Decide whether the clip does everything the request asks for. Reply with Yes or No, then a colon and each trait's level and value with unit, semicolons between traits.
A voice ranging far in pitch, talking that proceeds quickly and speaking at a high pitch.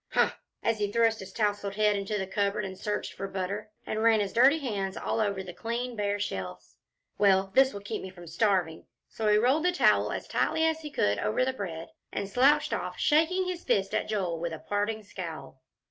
No: average, 3.4 semitones; fast, 215 wpm; high, 205 Hz